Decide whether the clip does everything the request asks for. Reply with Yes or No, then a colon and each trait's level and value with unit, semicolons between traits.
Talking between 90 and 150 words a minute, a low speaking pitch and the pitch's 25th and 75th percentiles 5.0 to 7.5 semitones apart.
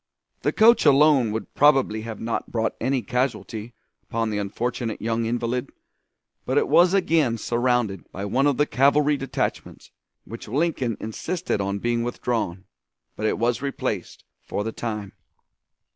No: average, 145 wpm; low, 120 Hz; average, 3.9 semitones